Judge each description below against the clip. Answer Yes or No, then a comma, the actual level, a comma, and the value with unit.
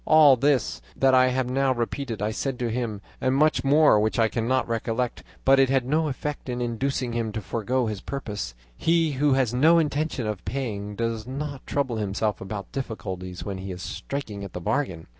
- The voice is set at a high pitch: No, low, 125 Hz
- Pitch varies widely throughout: No, average, 4.2 semitones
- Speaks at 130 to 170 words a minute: No, average, 195 wpm